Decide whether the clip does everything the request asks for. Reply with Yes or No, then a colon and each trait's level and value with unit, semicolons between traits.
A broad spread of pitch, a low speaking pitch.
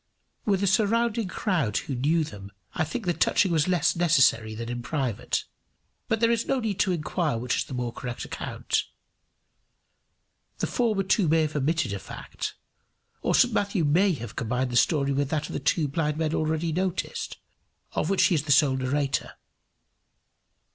No: wide, 6.1 semitones; medium, 155 Hz